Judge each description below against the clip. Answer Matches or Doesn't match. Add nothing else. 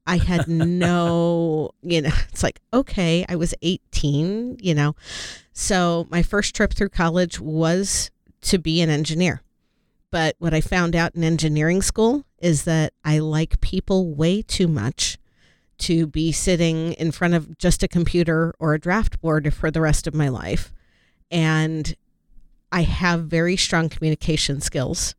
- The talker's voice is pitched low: Doesn't match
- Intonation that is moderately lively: Doesn't match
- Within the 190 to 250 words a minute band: Doesn't match